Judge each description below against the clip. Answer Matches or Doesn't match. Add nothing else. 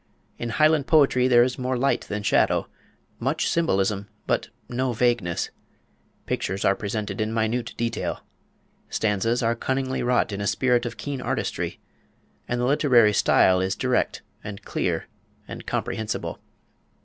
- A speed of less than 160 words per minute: Matches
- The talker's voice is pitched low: Matches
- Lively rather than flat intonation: Doesn't match